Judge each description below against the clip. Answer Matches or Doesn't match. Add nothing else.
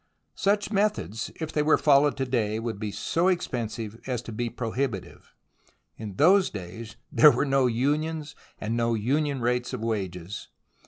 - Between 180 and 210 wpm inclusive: Doesn't match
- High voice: Doesn't match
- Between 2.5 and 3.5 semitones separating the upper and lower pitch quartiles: Doesn't match